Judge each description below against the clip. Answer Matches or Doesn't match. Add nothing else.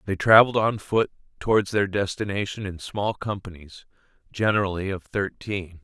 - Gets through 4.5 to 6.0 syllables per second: Matches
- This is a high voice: Doesn't match